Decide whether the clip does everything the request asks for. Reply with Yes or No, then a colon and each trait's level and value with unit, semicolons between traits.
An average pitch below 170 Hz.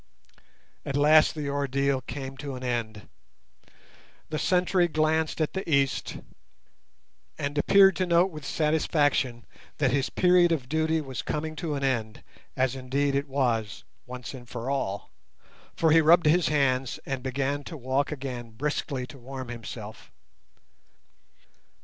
Yes: medium, 140 Hz